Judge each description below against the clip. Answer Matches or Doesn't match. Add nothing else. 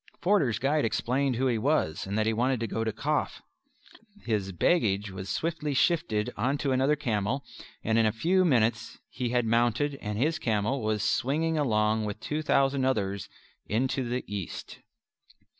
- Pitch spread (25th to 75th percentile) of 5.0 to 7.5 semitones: Doesn't match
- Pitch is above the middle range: Doesn't match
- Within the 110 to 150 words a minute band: Doesn't match